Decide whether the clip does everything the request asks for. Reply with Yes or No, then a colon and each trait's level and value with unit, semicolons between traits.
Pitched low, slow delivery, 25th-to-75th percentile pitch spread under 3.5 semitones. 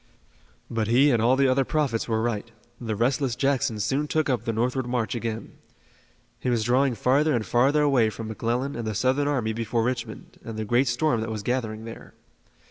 No: low, 120 Hz; average, 200 wpm; average, 2.9 semitones